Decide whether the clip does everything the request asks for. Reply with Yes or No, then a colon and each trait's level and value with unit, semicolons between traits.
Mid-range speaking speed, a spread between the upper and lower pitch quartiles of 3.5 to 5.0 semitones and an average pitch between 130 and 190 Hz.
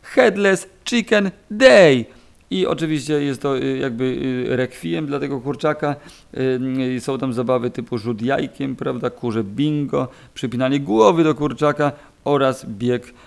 No: average, 120 wpm; average, 2.8 semitones; low, 135 Hz